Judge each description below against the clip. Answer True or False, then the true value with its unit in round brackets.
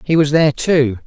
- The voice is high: False (145 Hz)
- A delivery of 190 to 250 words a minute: True (225 wpm)